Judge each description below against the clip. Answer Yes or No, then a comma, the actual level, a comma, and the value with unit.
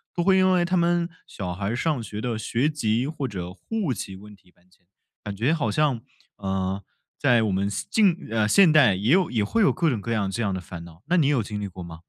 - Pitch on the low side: Yes, low, 115 Hz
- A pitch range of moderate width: No, wide, 8.1 semitones